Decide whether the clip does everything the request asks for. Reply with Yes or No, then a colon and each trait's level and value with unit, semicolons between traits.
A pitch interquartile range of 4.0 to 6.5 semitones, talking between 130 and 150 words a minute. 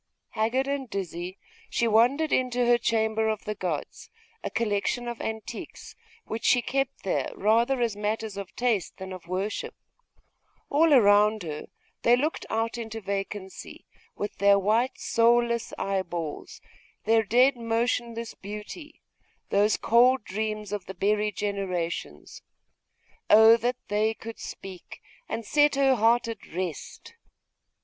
No: average, 3.0 semitones; slow, 135 wpm